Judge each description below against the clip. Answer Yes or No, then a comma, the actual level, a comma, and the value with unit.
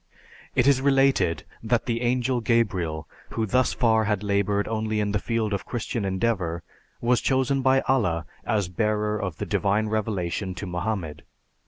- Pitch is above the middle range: No, low, 110 Hz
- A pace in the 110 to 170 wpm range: Yes, average, 160 wpm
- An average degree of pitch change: Yes, average, 3.7 semitones